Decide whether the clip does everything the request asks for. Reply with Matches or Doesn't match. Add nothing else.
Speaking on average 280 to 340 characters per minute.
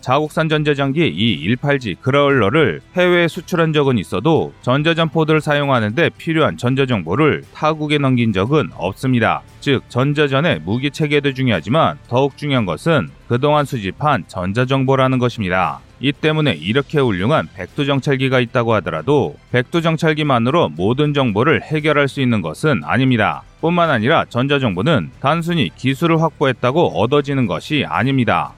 Doesn't match